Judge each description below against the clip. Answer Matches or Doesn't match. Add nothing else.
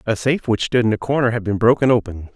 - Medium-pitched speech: Doesn't match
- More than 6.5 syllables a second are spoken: Matches